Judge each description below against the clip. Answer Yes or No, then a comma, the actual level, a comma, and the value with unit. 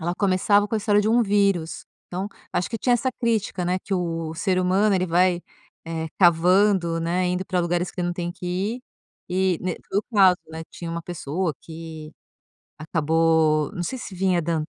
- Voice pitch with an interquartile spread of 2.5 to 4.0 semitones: Yes, average, 2.9 semitones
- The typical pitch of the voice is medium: Yes, medium, 180 Hz